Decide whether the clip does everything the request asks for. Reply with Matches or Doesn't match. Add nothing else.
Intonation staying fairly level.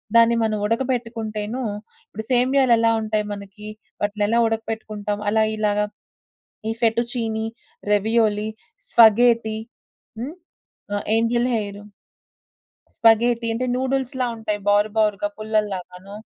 Matches